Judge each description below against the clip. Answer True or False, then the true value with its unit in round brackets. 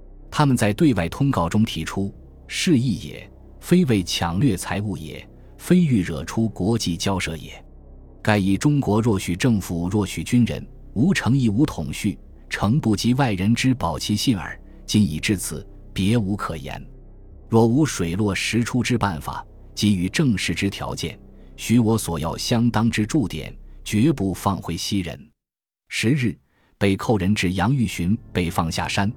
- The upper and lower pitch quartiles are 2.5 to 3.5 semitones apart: False (5.1 semitones)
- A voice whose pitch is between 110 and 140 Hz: False (100 Hz)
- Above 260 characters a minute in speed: False (225 characters per minute)